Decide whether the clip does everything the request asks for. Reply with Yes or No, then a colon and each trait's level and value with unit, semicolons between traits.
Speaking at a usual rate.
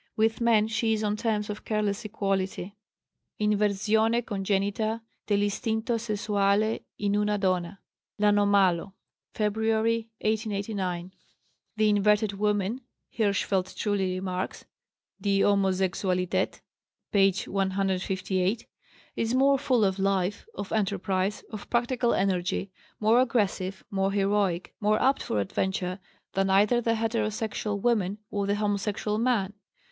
No: slow, 110 wpm